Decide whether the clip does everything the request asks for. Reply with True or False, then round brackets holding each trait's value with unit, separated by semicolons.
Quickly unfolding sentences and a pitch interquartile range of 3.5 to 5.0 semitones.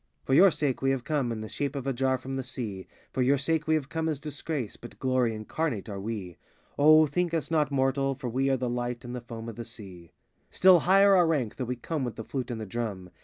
True (265 wpm; 4.1 semitones)